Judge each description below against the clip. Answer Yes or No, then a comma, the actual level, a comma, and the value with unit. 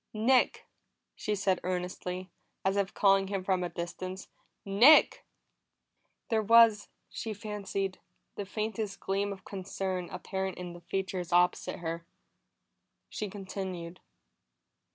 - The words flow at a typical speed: No, slow, 115 wpm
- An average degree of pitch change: No, narrow, 1.9 semitones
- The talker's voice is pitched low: No, high, 195 Hz